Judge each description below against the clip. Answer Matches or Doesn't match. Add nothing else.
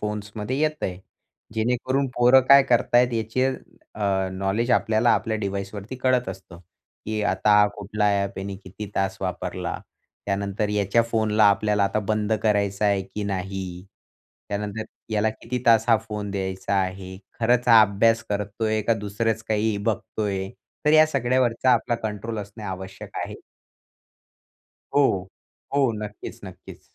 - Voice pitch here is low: Matches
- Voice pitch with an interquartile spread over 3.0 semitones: Doesn't match